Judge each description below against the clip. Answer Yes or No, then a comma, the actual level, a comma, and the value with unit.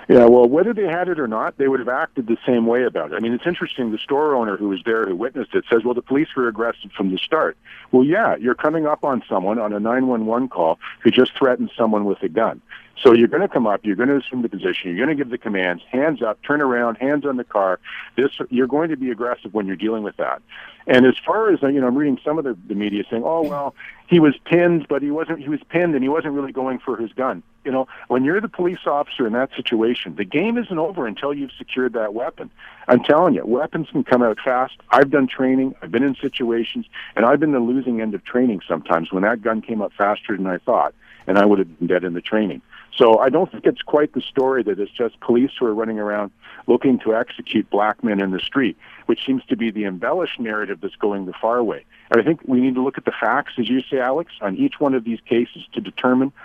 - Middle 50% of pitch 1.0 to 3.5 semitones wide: No, average, 4.4 semitones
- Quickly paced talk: Yes, fast, 265 wpm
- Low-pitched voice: Yes, low, 125 Hz